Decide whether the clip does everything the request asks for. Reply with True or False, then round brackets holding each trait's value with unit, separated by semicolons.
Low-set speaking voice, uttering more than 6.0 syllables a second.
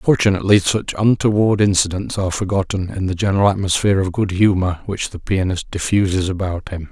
False (95 Hz; 5.9 syllables/s)